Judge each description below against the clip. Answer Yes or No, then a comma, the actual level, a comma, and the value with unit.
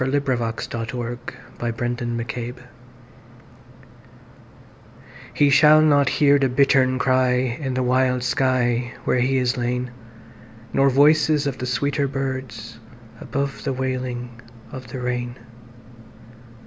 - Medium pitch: No, low, 125 Hz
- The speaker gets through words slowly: Yes, slow, 100 wpm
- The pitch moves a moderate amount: No, narrow, 2.0 semitones